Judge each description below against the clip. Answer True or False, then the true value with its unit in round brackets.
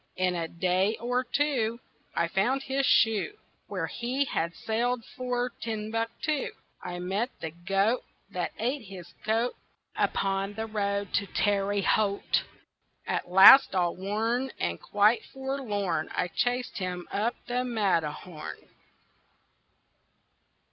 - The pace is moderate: False (120 wpm)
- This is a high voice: True (210 Hz)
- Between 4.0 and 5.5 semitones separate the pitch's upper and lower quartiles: True (4.7 semitones)